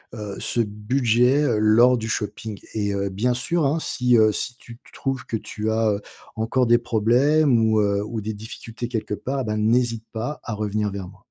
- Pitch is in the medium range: No, low, 110 Hz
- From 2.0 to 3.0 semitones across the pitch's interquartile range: Yes, narrow, 2.6 semitones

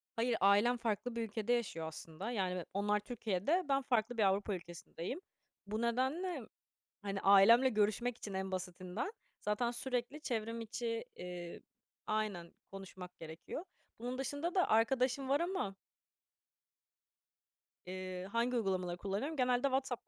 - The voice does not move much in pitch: No, average, 4.4 semitones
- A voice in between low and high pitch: No, high, 220 Hz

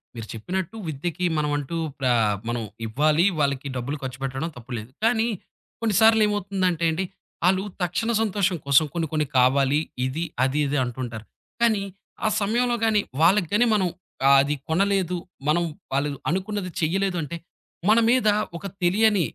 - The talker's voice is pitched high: No, medium, 170 Hz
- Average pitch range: No, wide, 6.3 semitones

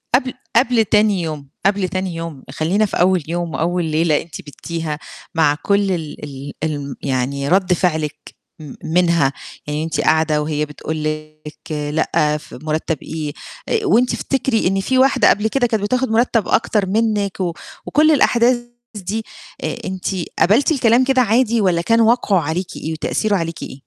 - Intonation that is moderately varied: No, wide, 6.2 semitones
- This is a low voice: No, medium, 175 Hz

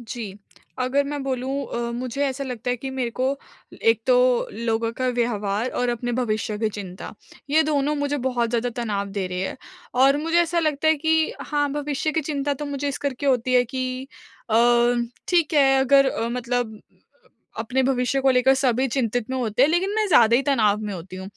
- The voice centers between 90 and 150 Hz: No, very high, 255 Hz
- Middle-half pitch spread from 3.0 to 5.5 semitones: Yes, average, 3.3 semitones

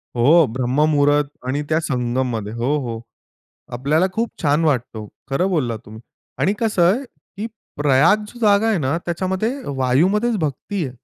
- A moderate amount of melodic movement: No, wide, 6.7 semitones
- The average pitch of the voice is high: No, medium, 150 Hz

